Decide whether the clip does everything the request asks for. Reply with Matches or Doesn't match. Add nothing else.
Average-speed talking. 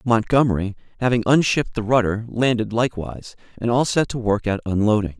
Matches